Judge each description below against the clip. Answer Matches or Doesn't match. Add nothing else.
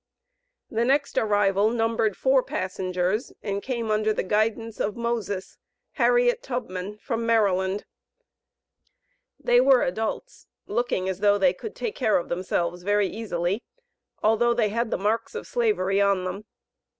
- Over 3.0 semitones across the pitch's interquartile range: Matches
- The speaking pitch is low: Doesn't match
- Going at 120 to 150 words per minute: Matches